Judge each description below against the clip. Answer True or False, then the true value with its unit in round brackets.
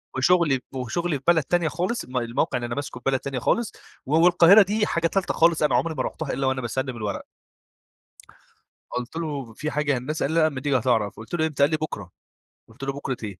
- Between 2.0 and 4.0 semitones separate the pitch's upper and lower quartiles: False (4.6 semitones)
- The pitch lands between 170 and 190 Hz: False (140 Hz)